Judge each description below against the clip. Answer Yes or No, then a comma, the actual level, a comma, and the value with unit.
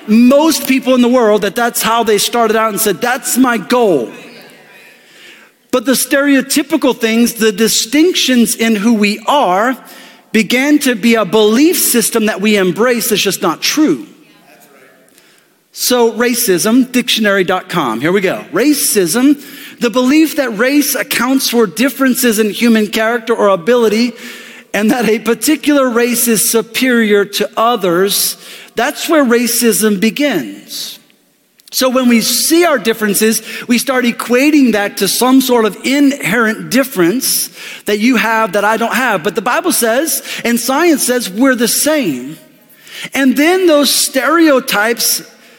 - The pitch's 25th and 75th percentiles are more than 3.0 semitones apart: Yes, average, 3.4 semitones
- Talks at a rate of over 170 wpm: No, average, 140 wpm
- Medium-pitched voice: No, high, 240 Hz